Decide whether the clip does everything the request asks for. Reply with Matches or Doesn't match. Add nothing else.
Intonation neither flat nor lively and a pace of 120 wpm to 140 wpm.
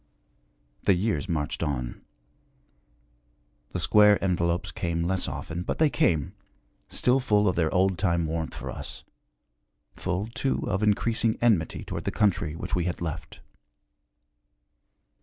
Matches